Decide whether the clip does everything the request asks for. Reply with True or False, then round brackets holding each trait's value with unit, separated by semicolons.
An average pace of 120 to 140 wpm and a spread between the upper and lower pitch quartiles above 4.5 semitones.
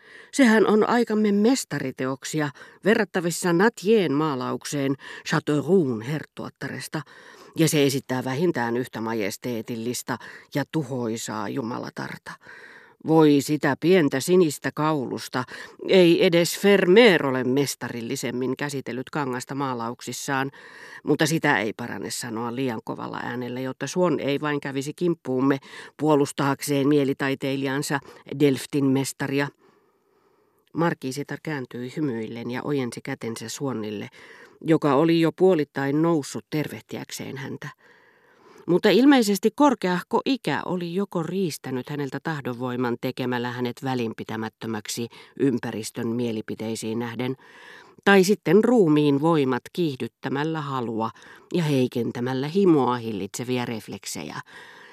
False (100 wpm; 5.1 semitones)